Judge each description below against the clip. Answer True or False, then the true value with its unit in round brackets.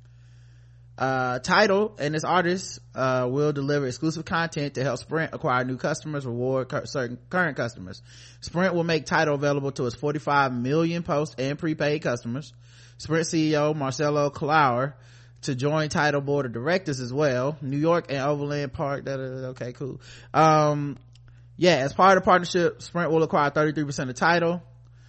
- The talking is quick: False (165 wpm)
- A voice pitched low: False (145 Hz)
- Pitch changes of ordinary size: True (4.0 semitones)